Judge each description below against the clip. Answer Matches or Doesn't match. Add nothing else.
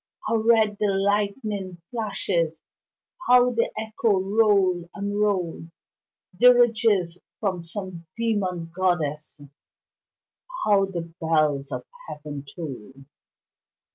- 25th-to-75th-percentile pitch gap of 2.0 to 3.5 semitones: Doesn't match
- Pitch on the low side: Doesn't match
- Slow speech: Matches